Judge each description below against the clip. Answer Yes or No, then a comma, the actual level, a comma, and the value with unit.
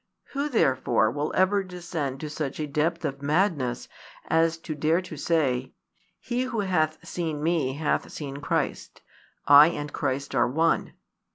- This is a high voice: No, medium, 155 Hz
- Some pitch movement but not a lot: Yes, average, 3.4 semitones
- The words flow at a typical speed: Yes, average, 155 wpm